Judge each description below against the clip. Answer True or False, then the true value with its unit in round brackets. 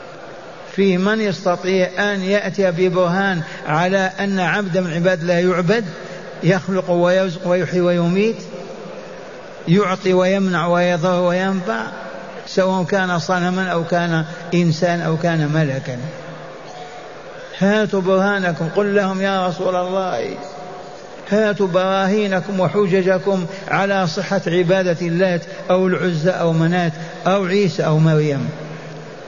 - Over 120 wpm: False (105 wpm)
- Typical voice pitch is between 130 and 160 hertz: False (185 Hz)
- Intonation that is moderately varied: False (1.7 semitones)